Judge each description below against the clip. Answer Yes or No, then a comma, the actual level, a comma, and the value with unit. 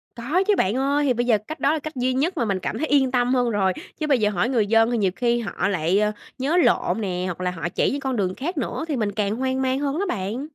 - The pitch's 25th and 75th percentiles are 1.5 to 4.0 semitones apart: No, average, 5.2 semitones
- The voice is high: Yes, high, 245 Hz